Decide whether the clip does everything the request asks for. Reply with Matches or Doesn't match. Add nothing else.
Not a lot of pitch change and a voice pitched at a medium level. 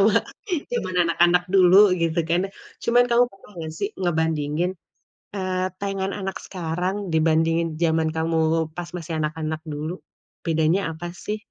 Doesn't match